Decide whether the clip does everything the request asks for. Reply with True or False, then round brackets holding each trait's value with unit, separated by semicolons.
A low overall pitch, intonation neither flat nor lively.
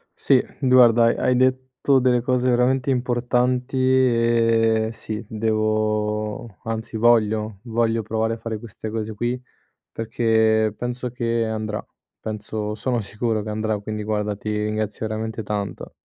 False (110 Hz; 2.1 semitones)